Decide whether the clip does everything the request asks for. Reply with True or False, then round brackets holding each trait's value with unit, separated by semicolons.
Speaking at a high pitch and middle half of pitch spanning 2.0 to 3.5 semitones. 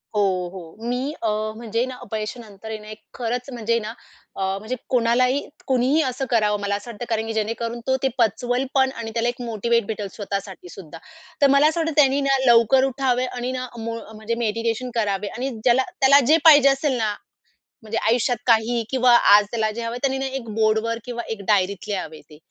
True (235 Hz; 2.9 semitones)